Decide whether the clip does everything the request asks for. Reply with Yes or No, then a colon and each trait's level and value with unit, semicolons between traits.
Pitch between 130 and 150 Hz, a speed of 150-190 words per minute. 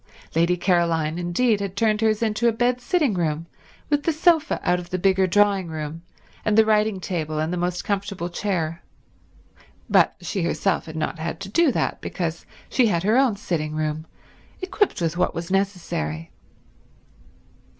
No: medium, 185 Hz; average, 170 wpm